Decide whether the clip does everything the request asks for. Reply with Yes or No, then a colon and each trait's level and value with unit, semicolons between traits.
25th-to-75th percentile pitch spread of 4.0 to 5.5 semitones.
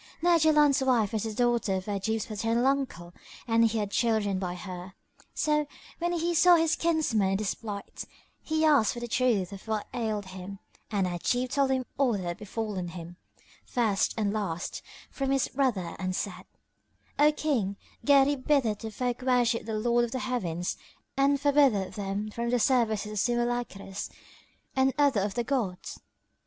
Yes: average, 5.0 semitones